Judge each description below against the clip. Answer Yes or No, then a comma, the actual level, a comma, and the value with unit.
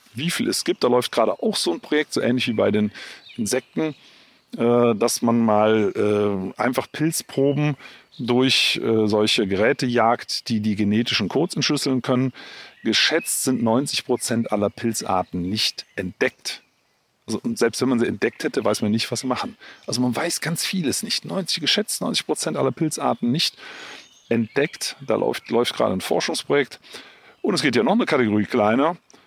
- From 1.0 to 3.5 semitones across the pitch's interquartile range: No, average, 5.2 semitones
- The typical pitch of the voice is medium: No, low, 120 Hz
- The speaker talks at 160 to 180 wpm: Yes, average, 165 wpm